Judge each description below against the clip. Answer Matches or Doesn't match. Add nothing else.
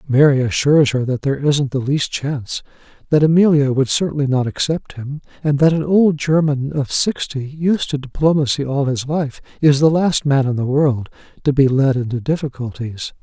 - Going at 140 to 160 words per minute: Doesn't match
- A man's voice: Matches